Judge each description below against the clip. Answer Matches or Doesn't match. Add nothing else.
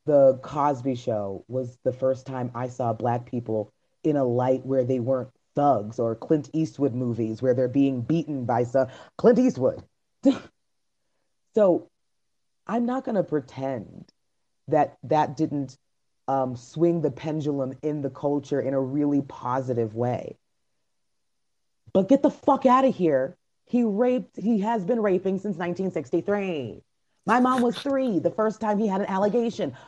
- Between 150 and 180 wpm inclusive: Matches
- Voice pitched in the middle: Matches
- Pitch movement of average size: Doesn't match